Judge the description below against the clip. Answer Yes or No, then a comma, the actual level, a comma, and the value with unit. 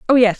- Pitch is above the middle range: Yes, high, 230 Hz